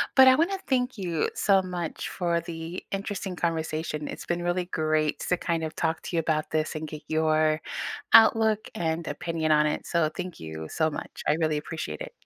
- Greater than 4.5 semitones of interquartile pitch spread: No, average, 2.9 semitones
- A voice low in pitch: No, medium, 165 Hz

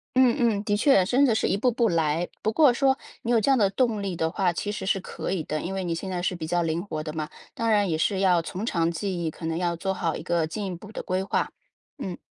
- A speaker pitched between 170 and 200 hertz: Yes, high, 190 Hz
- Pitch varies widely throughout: No, average, 4.2 semitones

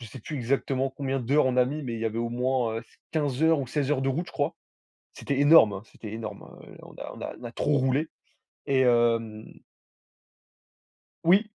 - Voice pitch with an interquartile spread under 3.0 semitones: No, average, 3.5 semitones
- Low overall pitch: Yes, low, 130 Hz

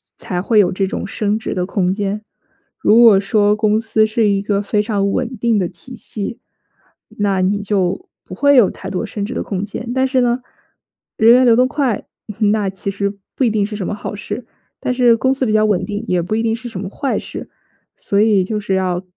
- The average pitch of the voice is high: Yes, high, 210 Hz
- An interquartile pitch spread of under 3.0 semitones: Yes, narrow, 2.6 semitones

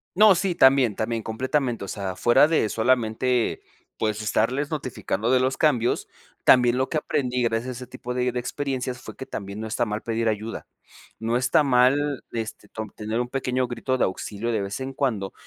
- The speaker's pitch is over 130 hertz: No, low, 125 Hz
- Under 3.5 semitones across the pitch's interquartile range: Yes, average, 2.9 semitones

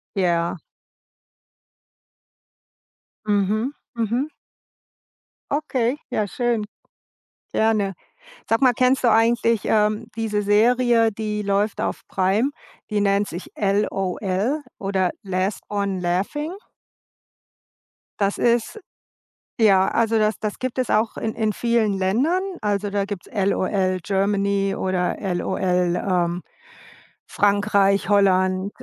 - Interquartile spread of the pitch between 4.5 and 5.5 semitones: No, average, 2.7 semitones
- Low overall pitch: No, high, 205 Hz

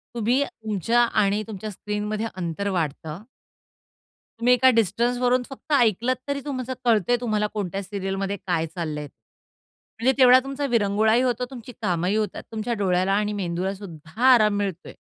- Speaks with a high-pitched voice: Yes, high, 210 Hz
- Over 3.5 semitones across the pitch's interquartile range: Yes, average, 4.1 semitones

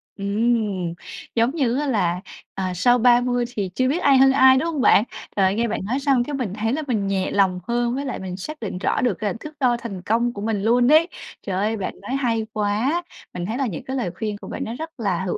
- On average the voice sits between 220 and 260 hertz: Yes, high, 230 Hz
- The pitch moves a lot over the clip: No, average, 4.5 semitones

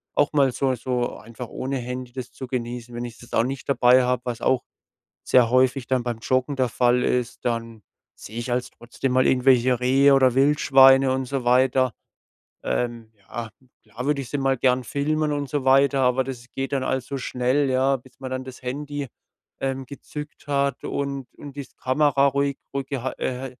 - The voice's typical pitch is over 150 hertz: No, low, 130 Hz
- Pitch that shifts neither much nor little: No, narrow, 1.8 semitones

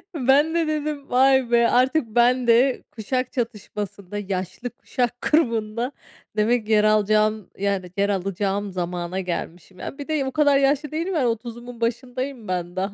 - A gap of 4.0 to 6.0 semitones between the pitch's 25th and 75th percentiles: Yes, average, 4.7 semitones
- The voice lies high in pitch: Yes, high, 235 Hz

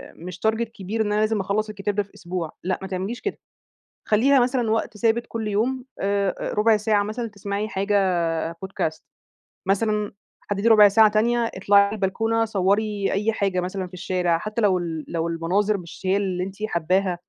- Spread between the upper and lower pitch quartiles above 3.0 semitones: No, average, 2.7 semitones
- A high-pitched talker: Yes, high, 205 Hz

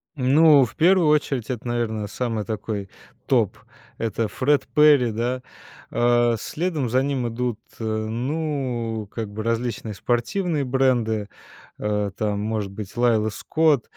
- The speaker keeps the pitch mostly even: No, average, 3.8 semitones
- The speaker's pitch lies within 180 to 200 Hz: No, low, 120 Hz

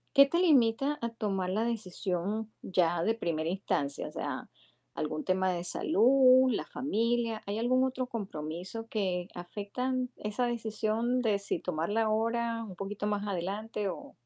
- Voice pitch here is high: Yes, high, 215 Hz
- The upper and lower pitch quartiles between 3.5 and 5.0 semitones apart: Yes, average, 4.1 semitones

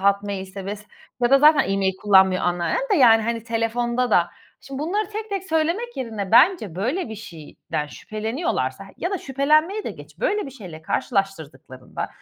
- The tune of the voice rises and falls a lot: Yes, wide, 8.0 semitones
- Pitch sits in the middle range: No, high, 230 Hz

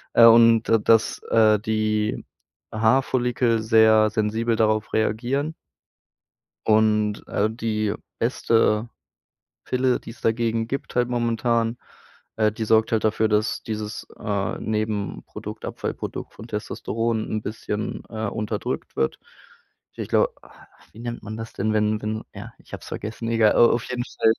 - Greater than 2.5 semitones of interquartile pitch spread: No, narrow, 1.3 semitones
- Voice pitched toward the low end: Yes, low, 110 Hz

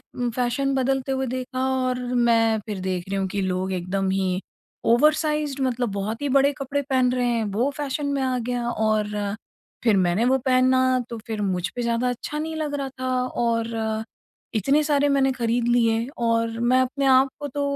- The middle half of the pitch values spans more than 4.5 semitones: No, average, 3.2 semitones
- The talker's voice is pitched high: Yes, high, 245 Hz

